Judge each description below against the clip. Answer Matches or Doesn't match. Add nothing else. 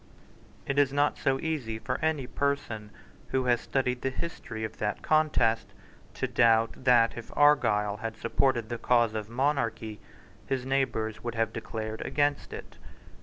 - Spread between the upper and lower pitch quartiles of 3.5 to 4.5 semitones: Matches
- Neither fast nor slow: Matches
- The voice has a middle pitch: Doesn't match